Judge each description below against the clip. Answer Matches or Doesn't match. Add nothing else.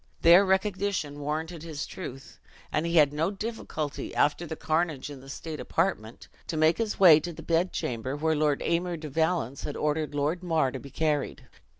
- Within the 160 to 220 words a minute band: Matches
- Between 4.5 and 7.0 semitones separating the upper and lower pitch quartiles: Doesn't match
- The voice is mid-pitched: Matches